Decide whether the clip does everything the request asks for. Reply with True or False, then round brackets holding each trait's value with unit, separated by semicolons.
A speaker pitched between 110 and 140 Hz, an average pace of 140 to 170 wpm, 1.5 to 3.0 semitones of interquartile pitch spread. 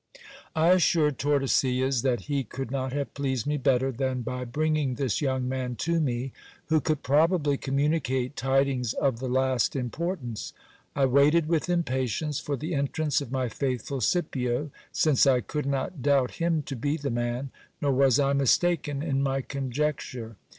True (135 Hz; 165 wpm; 2.6 semitones)